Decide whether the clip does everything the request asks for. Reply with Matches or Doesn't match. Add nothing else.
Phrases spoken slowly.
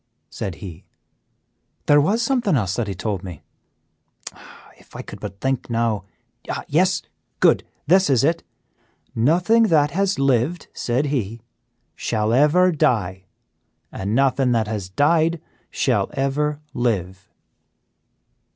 Matches